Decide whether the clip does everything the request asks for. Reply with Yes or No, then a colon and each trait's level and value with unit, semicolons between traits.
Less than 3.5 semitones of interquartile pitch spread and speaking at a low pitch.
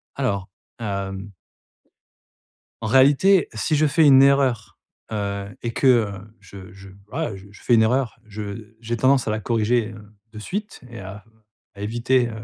No: average, 4.5 semitones; low, 115 Hz